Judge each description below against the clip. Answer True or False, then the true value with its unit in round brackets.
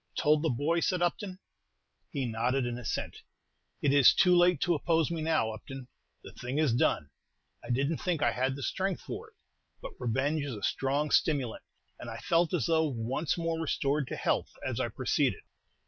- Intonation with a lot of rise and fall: False (4.8 semitones)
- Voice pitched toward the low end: False (145 Hz)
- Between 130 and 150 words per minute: False (185 wpm)